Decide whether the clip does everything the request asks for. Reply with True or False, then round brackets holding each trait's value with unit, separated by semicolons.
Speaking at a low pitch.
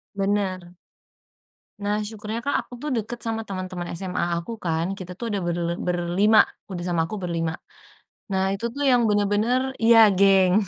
False (195 Hz)